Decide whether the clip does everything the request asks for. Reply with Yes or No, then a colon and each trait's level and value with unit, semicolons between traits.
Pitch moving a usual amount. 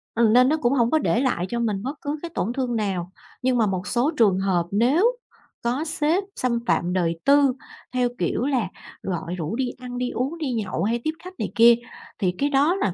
No: wide, 5.8 semitones